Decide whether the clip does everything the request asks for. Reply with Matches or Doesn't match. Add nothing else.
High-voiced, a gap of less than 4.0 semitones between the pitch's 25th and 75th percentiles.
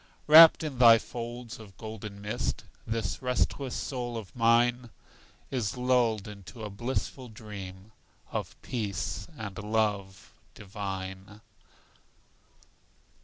Doesn't match